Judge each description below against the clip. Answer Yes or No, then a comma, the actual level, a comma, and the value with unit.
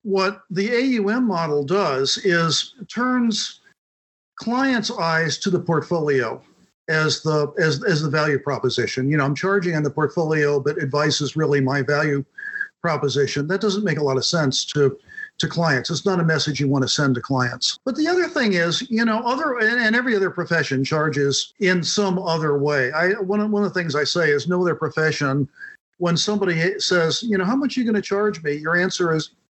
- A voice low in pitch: No, medium, 170 Hz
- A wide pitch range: Yes, wide, 5.8 semitones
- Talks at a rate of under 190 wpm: No, fast, 205 wpm